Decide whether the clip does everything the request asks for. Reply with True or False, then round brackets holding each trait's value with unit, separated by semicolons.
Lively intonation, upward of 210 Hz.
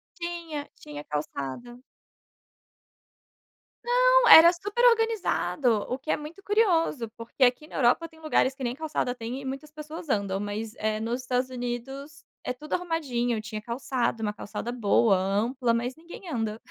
True (5.8 semitones; 255 Hz)